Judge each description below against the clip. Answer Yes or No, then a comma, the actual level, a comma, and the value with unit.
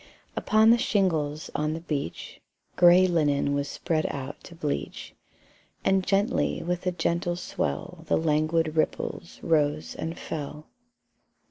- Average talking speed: No, slow, 130 wpm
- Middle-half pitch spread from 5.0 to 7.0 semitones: No, average, 2.9 semitones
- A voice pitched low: No, medium, 165 Hz